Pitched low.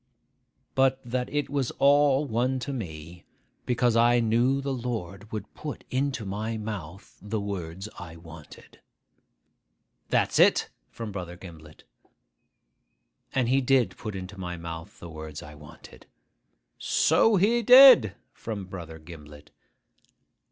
Yes: low, 105 Hz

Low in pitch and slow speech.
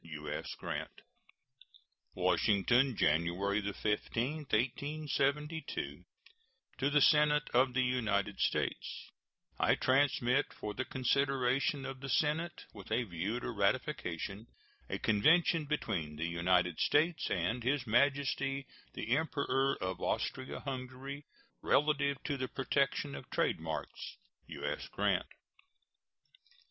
Yes: low, 130 Hz; slow, 110 wpm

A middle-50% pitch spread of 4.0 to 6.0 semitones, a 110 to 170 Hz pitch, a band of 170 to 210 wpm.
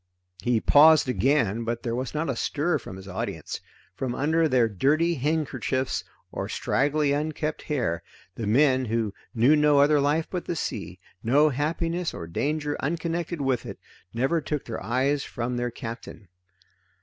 No: average, 4.4 semitones; medium, 140 Hz; average, 160 wpm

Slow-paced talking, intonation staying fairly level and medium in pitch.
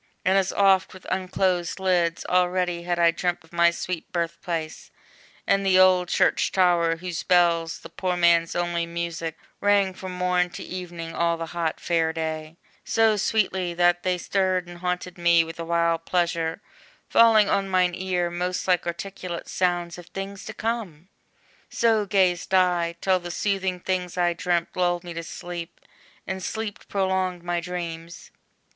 No: average, 165 wpm; narrow, 1.7 semitones; medium, 175 Hz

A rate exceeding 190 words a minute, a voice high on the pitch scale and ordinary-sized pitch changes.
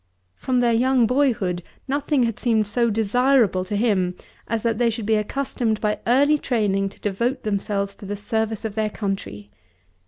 No: average, 175 wpm; high, 220 Hz; average, 3.4 semitones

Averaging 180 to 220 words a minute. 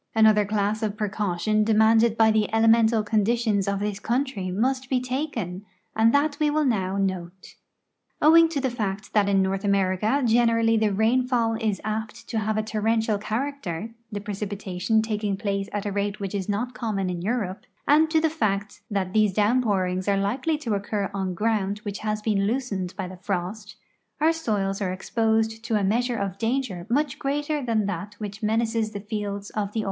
Yes: average, 185 wpm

